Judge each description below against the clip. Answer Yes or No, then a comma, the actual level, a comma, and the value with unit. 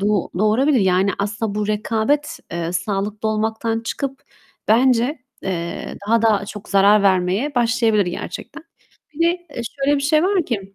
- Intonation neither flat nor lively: Yes, average, 4.5 semitones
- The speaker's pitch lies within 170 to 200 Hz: No, high, 220 Hz